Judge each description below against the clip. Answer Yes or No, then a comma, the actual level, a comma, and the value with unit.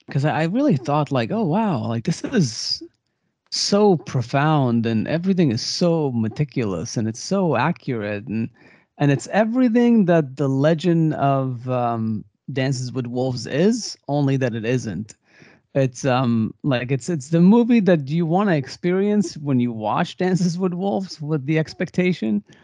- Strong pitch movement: Yes, wide, 6.2 semitones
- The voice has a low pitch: No, medium, 145 Hz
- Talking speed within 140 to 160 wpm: Yes, average, 155 wpm